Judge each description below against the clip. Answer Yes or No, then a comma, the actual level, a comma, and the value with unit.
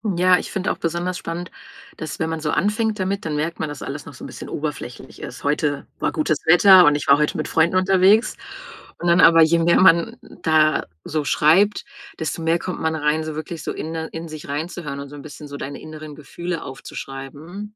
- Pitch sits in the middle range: Yes, medium, 160 Hz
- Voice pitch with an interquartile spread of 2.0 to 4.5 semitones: Yes, average, 2.8 semitones